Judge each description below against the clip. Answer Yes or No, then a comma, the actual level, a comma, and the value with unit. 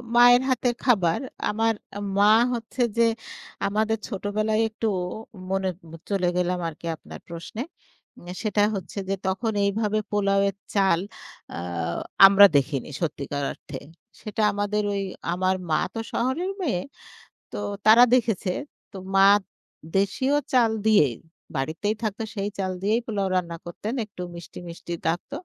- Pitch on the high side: Yes, high, 205 Hz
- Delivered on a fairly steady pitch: No, average, 3.4 semitones